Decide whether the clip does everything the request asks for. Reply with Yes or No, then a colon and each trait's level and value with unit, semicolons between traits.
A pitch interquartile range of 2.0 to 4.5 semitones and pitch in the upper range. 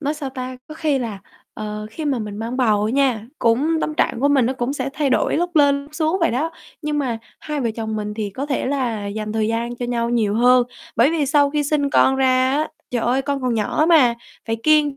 Yes: average, 4.2 semitones; very high, 260 Hz